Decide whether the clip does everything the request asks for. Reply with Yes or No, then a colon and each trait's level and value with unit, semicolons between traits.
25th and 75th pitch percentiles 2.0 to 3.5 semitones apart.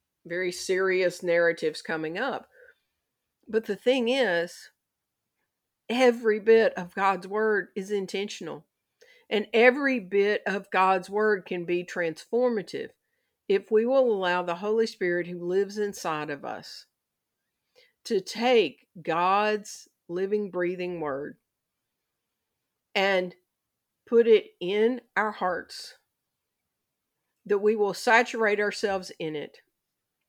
No: average, 4.0 semitones